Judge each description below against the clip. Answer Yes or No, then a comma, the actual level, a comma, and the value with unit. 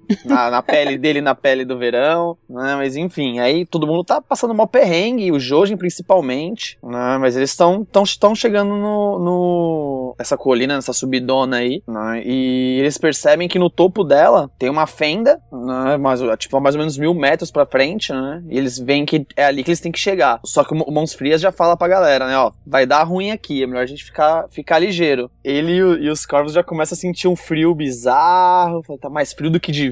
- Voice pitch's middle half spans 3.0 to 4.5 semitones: No, average, 4.9 semitones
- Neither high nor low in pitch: Yes, medium, 150 Hz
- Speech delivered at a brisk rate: Yes, fast, 220 wpm